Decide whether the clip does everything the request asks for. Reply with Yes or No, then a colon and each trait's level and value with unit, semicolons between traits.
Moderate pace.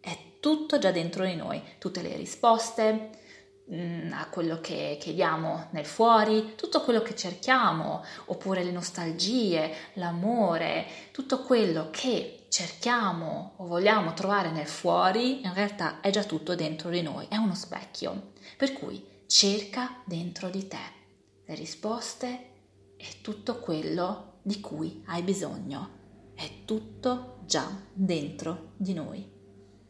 Yes: average, 130 wpm